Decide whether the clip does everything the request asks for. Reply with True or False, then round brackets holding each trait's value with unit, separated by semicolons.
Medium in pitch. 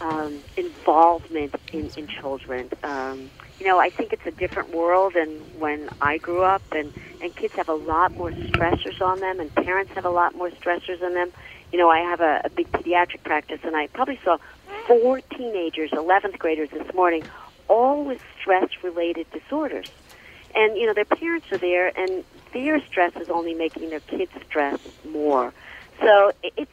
True (180 Hz)